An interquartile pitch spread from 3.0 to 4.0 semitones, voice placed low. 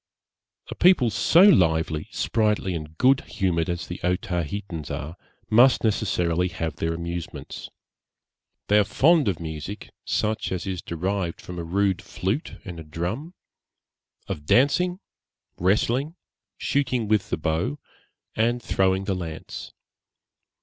No: average, 5.0 semitones; very low, 95 Hz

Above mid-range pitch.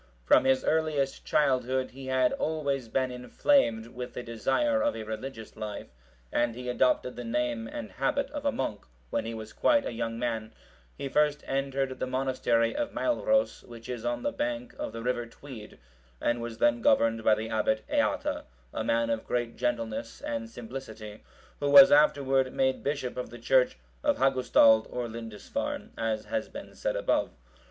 No: low, 125 Hz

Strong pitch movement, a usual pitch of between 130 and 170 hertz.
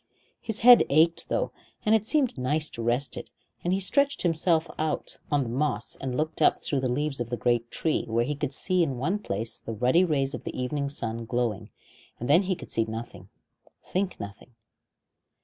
Yes: wide, 6.2 semitones; medium, 140 Hz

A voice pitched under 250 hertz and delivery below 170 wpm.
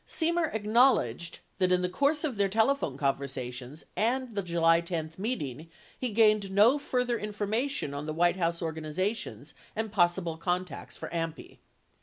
Yes: medium, 185 Hz; average, 150 wpm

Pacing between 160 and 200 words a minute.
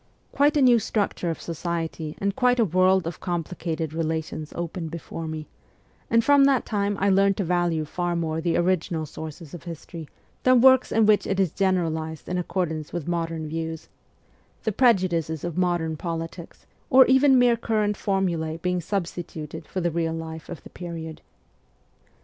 Yes: average, 175 wpm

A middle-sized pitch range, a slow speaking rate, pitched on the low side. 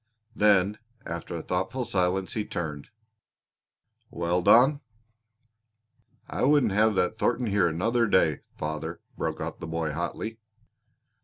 Yes: average, 4.7 semitones; slow, 125 wpm; very low, 95 Hz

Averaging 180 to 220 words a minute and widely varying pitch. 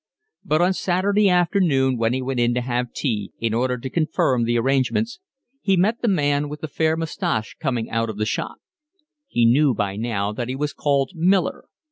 Yes: average, 195 wpm; wide, 6.0 semitones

